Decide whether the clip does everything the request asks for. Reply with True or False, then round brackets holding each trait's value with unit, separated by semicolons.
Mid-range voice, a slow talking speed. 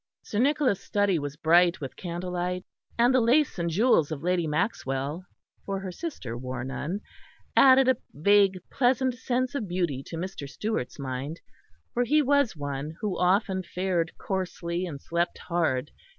False (180 Hz; 155 wpm)